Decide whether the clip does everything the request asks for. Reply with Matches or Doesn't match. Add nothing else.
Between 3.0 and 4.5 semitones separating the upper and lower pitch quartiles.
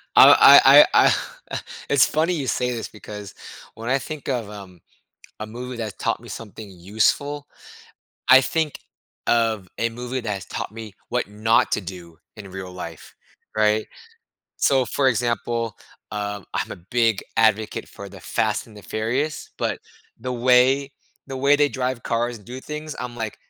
Matches